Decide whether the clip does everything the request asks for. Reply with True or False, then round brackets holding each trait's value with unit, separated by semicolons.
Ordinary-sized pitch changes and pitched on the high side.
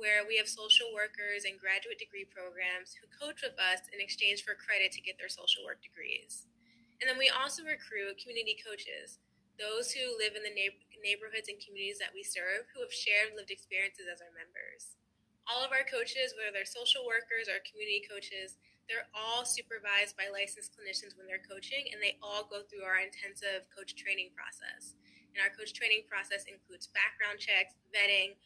True (4.7 semitones; 210 Hz)